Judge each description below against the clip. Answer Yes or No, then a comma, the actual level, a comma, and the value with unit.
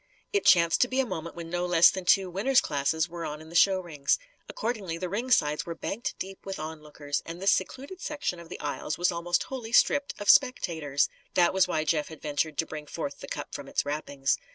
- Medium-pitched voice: Yes, medium, 170 Hz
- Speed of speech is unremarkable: No, fast, 225 wpm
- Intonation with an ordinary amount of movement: Yes, average, 3.9 semitones